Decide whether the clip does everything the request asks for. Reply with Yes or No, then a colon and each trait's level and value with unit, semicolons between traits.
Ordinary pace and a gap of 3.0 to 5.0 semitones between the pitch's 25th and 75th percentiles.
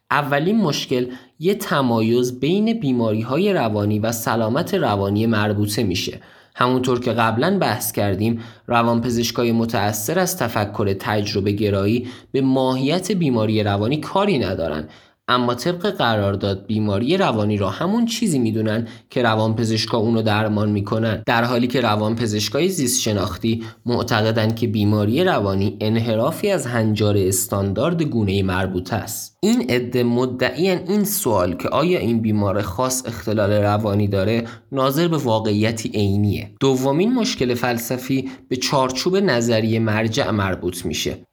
Yes: average, 130 wpm; average, 3.7 semitones